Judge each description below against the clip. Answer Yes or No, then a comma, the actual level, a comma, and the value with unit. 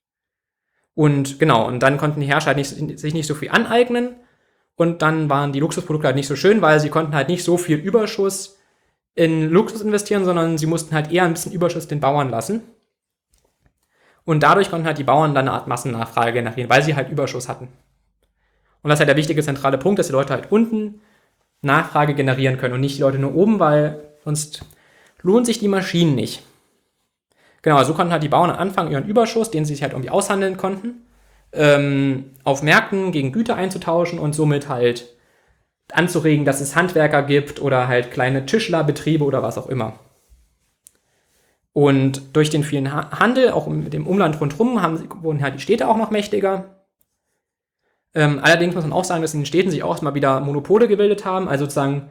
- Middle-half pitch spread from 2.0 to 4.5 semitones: No, average, 5.2 semitones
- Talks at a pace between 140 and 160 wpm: No, average, 185 wpm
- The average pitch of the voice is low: No, medium, 155 Hz